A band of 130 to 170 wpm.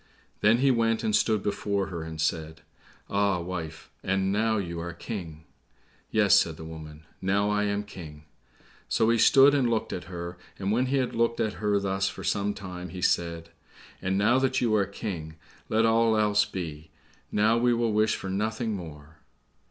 No: average, 185 wpm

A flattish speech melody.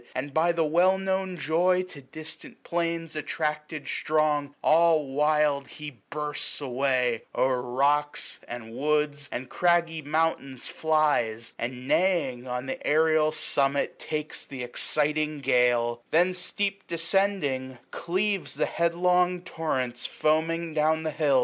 No: average, 3.7 semitones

